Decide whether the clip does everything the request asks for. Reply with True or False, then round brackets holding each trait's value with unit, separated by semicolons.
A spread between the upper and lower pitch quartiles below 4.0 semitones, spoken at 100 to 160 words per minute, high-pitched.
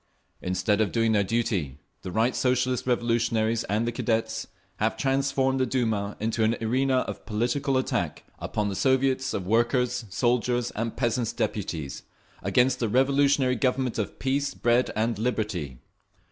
False (2.8 semitones; 145 wpm; 120 Hz)